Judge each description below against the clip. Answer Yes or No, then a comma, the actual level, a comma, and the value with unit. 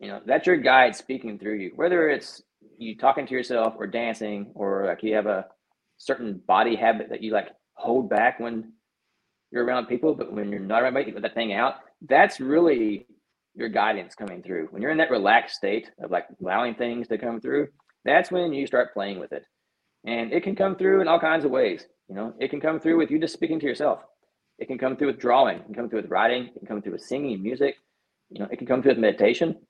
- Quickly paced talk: Yes, fast, 240 wpm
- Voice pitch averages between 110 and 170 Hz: Yes, low, 125 Hz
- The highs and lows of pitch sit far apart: Yes, wide, 5.9 semitones